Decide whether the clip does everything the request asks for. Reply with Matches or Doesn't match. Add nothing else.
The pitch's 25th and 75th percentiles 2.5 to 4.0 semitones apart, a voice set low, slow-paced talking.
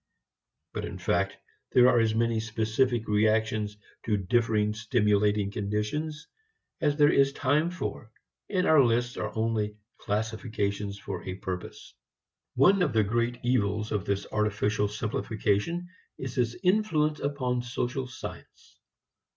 Matches